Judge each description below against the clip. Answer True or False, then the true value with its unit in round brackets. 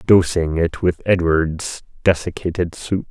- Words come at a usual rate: False (115 wpm)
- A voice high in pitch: False (85 Hz)